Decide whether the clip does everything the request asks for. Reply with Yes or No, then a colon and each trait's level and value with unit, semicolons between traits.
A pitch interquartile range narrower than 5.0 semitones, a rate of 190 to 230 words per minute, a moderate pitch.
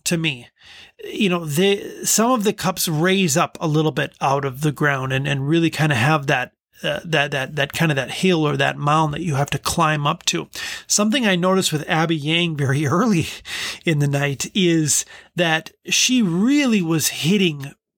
Yes: average, 4.3 semitones; fast, 205 wpm; medium, 160 Hz